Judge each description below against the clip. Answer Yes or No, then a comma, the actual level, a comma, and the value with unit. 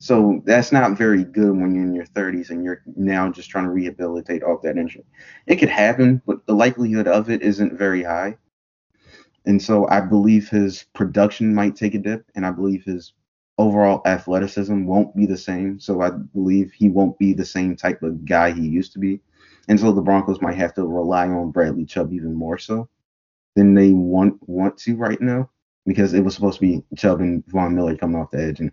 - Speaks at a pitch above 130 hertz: No, very low, 95 Hz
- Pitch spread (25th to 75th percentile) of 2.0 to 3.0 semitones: Yes, narrow, 2.4 semitones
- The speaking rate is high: Yes, fast, 215 wpm